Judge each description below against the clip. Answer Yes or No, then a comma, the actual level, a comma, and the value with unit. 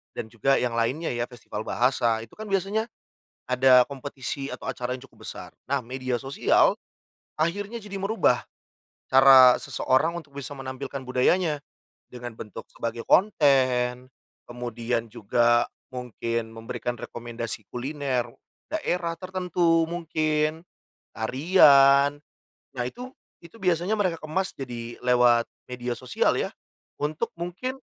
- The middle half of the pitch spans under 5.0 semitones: No, wide, 5.4 semitones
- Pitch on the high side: No, low, 135 Hz